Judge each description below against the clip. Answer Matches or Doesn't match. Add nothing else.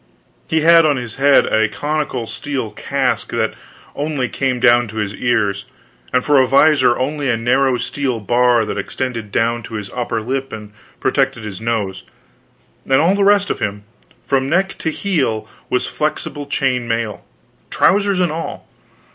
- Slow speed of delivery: Doesn't match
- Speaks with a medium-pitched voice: Doesn't match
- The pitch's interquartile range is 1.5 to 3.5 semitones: Doesn't match